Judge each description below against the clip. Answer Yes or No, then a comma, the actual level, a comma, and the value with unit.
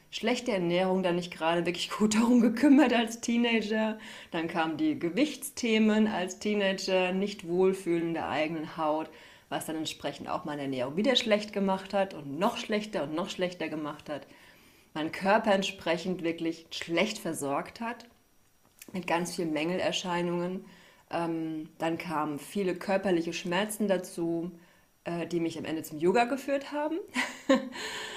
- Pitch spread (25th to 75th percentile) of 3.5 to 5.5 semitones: Yes, average, 4.6 semitones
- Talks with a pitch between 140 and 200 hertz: Yes, medium, 185 Hz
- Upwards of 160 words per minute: No, average, 140 wpm